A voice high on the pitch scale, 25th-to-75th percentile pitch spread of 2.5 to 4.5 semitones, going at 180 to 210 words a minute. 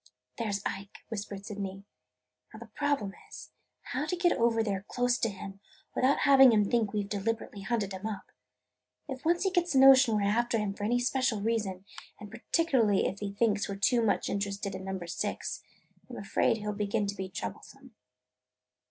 Yes: high, 215 Hz; average, 3.5 semitones; average, 200 wpm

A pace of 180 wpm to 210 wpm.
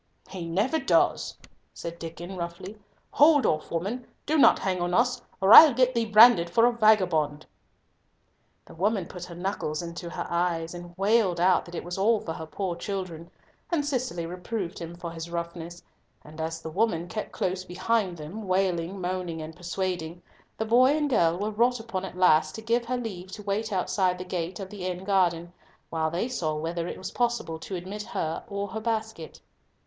Yes: average, 190 wpm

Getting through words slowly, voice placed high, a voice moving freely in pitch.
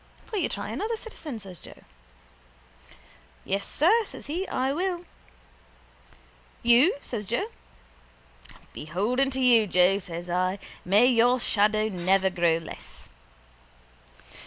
Yes: slow, 115 wpm; high, 220 Hz; wide, 6.6 semitones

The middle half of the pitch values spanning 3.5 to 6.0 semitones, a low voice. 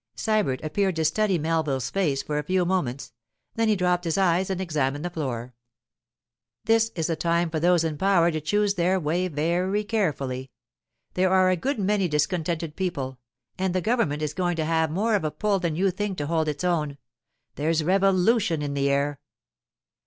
No: average, 4.0 semitones; medium, 170 Hz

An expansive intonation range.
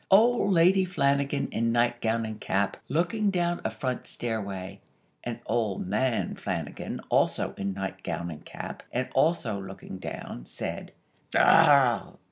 Yes: wide, 8.5 semitones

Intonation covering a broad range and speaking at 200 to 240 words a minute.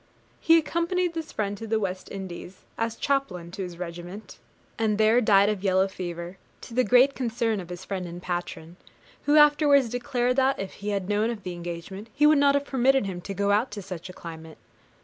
Yes: wide, 5.8 semitones; fast, 205 wpm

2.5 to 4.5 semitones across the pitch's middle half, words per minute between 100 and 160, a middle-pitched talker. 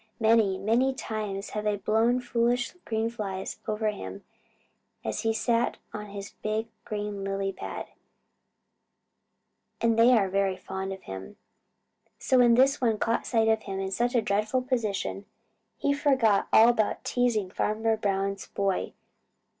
No: average, 2.9 semitones; average, 150 wpm; high, 215 Hz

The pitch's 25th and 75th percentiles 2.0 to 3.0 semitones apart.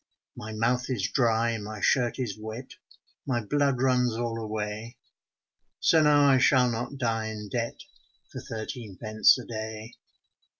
Yes: average, 2.7 semitones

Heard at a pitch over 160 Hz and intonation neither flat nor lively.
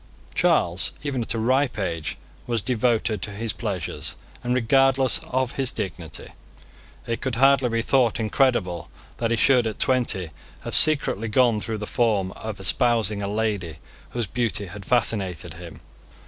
No: low, 115 Hz; average, 3.7 semitones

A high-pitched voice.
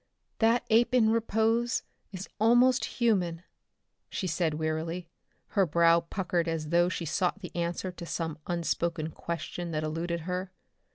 No: medium, 175 Hz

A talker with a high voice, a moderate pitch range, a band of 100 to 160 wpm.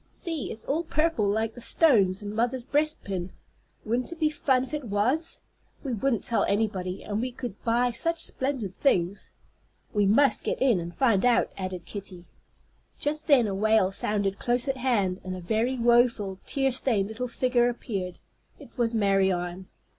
No: high, 230 Hz; average, 4.9 semitones; average, 170 wpm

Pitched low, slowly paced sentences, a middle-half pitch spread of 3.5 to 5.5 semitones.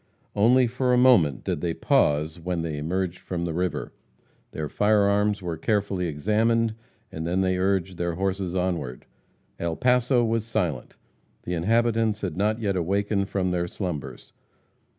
No: very low, 95 Hz; average, 155 wpm; average, 4.1 semitones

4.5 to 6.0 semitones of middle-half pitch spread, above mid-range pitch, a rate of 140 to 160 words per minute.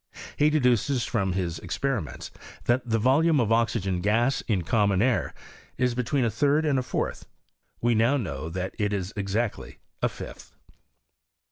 No: average, 4.8 semitones; low, 115 Hz; average, 155 wpm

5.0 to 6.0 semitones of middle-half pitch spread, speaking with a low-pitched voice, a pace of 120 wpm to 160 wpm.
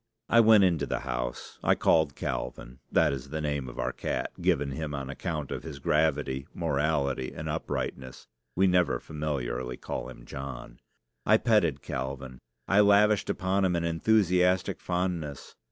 Yes: wide, 5.4 semitones; very low, 75 Hz; average, 155 wpm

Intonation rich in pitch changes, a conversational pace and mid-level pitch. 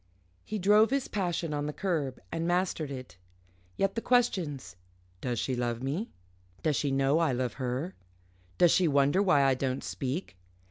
Yes: wide, 5.7 semitones; average, 170 wpm; medium, 150 Hz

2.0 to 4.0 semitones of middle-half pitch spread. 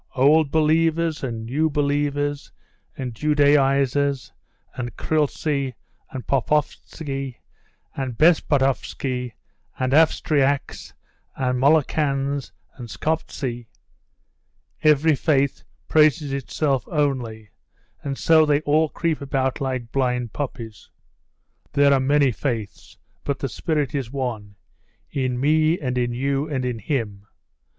Yes: average, 2.8 semitones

